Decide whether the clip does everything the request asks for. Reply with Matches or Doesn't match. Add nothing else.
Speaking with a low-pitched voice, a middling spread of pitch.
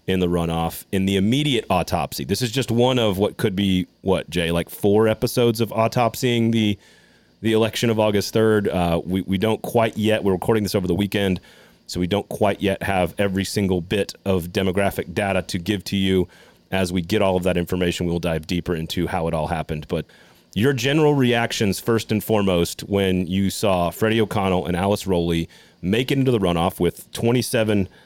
Matches